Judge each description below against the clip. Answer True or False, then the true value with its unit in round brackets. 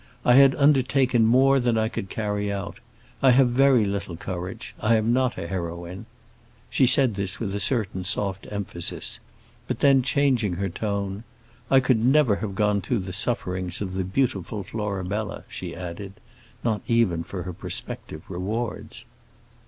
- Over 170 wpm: False (160 wpm)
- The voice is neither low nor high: False (105 Hz)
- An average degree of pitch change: True (4.4 semitones)